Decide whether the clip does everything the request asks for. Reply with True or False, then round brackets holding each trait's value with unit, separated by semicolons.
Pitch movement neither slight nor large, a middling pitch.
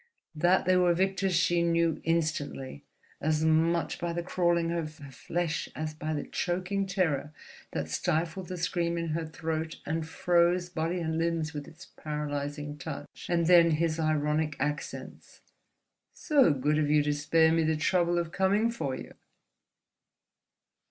False (2.2 semitones; 165 Hz)